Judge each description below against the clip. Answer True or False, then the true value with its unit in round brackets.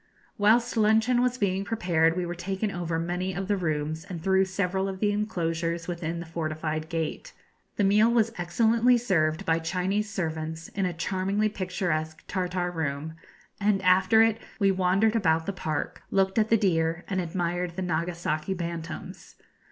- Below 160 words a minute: False (165 wpm)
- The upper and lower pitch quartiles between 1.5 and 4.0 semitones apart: True (3.6 semitones)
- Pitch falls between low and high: True (180 Hz)